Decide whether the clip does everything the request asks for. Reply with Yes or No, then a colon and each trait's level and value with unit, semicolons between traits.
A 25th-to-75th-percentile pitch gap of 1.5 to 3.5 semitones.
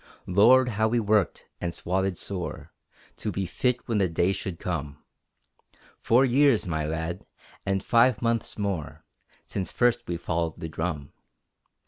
No: wide, 5.4 semitones